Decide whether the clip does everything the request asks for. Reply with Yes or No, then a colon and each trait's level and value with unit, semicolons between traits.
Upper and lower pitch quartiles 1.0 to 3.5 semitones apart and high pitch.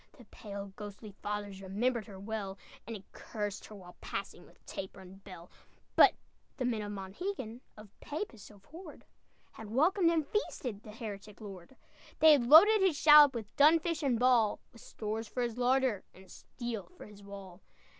No: average, 4.8 semitones; high, 220 Hz